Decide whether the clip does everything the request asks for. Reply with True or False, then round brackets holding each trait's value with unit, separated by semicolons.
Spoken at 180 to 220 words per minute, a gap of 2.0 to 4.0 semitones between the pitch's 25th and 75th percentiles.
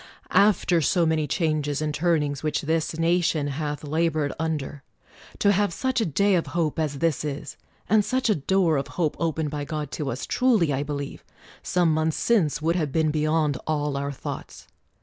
True (185 wpm; 2.5 semitones)